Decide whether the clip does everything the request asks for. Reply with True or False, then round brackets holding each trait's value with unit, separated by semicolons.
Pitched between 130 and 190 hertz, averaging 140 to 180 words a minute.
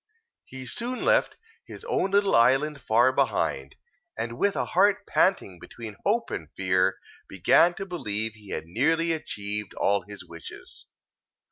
False (120 Hz; 145 wpm)